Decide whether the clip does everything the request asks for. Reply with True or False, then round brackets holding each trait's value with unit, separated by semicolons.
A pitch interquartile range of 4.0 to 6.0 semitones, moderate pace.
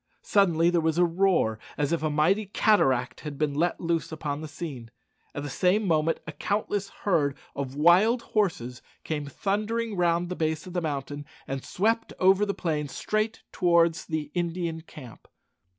True (4.3 semitones; 170 wpm)